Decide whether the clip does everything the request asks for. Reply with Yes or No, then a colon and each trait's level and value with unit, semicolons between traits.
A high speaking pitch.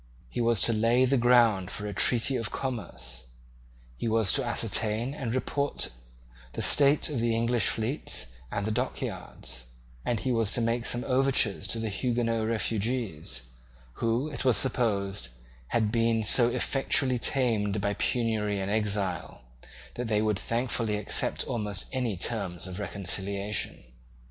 No: low, 115 Hz